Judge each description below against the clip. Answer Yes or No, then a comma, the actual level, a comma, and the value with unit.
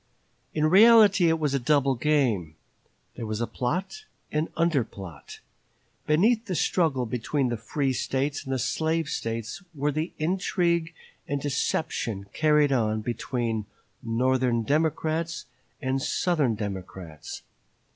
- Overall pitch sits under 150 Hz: Yes, medium, 140 Hz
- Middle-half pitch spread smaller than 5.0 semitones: No, wide, 5.5 semitones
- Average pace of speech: No, slow, 125 wpm